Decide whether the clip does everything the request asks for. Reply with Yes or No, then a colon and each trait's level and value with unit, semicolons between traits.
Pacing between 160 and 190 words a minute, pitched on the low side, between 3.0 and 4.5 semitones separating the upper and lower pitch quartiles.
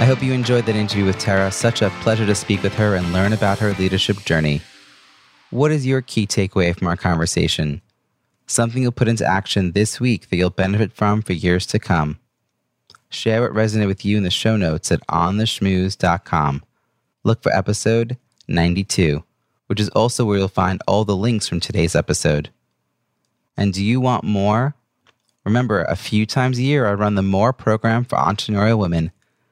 Yes: average, 185 wpm; low, 105 Hz; average, 3.4 semitones